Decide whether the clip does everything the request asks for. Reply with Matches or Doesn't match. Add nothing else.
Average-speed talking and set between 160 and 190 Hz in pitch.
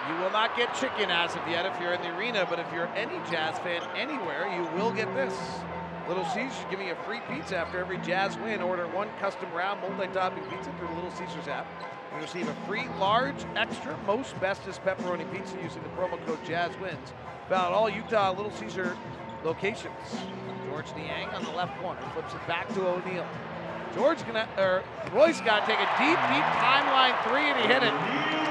Matches